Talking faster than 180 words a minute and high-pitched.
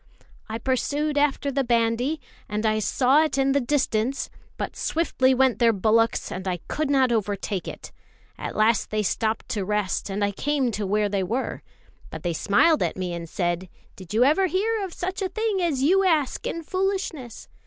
Yes: average, 190 wpm; very high, 250 Hz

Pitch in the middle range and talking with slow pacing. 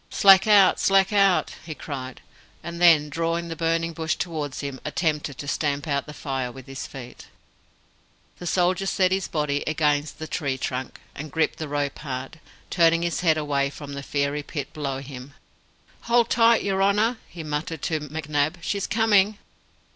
No: medium, 155 Hz; average, 170 wpm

